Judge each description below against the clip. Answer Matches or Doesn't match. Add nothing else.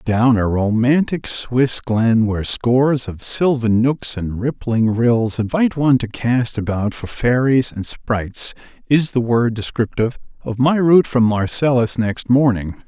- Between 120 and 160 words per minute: Matches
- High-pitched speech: Doesn't match